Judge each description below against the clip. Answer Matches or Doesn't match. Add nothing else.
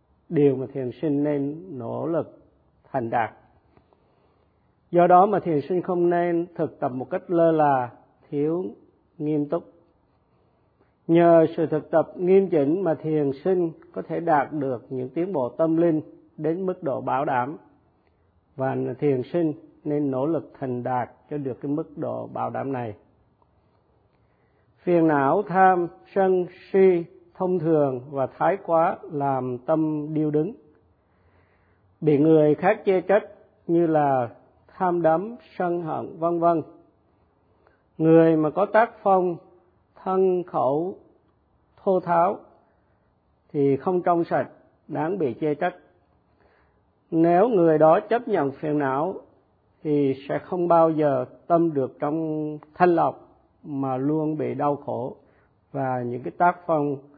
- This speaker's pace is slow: Matches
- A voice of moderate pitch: Matches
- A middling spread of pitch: Matches